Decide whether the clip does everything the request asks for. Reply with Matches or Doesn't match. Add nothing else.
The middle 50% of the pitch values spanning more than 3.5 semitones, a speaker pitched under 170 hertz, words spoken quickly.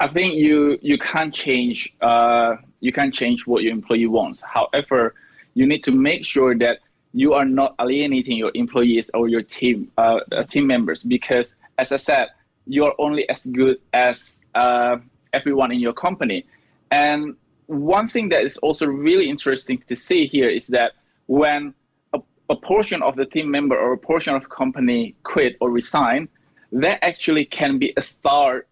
Doesn't match